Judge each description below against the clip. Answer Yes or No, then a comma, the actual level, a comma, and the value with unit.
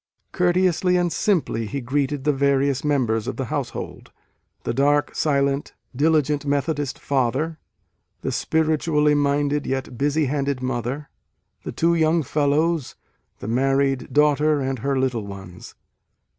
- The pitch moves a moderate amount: No, narrow, 2.3 semitones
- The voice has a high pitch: No, medium, 140 Hz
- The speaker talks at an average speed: No, slow, 130 wpm